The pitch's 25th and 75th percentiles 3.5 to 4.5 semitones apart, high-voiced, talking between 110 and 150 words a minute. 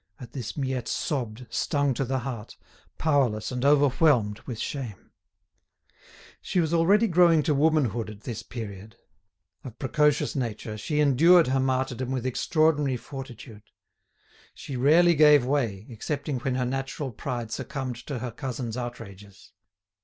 No: average, 3.9 semitones; low, 130 Hz; average, 140 wpm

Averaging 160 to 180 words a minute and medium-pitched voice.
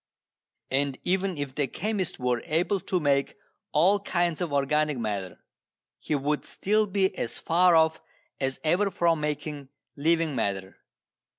No: average, 140 wpm; medium, 155 Hz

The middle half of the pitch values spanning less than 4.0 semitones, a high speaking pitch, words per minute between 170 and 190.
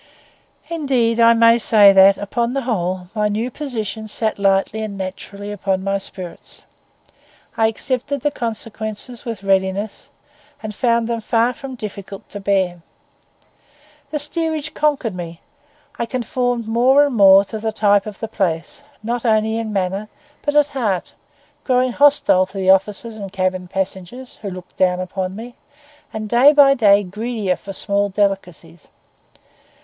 No: average, 3.6 semitones; high, 215 Hz; average, 150 wpm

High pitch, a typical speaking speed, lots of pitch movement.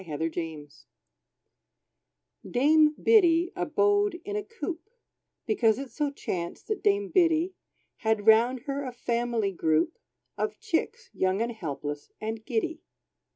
No: very high, 260 Hz; slow, 125 wpm; wide, 8.6 semitones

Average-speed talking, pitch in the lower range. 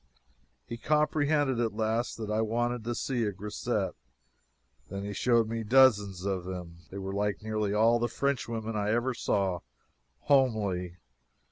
Yes: average, 150 wpm; low, 110 Hz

